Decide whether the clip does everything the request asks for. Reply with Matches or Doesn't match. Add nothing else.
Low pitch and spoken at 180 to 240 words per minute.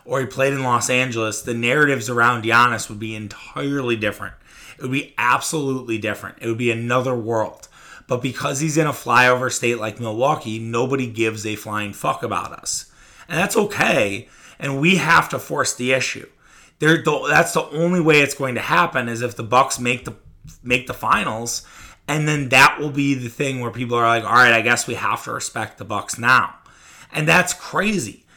Matches